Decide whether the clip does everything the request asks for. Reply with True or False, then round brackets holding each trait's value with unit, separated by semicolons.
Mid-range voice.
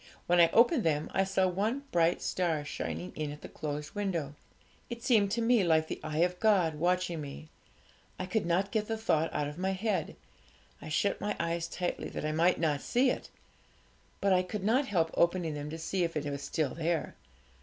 True (175 Hz)